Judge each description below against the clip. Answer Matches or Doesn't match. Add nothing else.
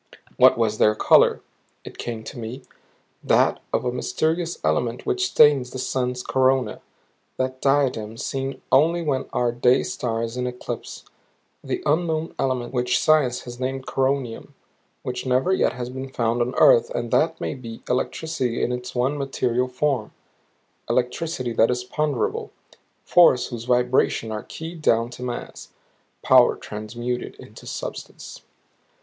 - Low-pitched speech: Matches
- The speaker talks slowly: Doesn't match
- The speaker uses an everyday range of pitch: Doesn't match